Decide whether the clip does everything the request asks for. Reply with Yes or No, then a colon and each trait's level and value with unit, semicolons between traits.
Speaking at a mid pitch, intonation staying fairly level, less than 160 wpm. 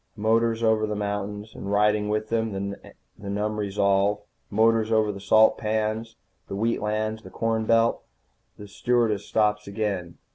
No: low, 105 Hz; narrow, 1.4 semitones; average, 150 wpm